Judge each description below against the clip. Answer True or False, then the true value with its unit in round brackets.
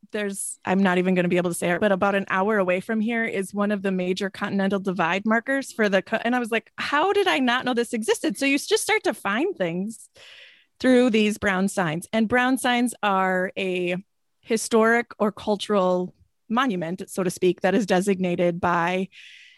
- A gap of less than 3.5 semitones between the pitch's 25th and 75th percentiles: False (4.5 semitones)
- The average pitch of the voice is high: True (205 Hz)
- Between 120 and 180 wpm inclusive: False (205 wpm)